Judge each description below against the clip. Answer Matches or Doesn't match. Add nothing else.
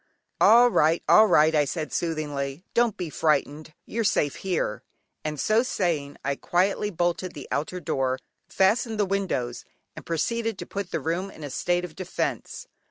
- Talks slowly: Doesn't match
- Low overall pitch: Doesn't match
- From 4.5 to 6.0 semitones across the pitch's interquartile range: Matches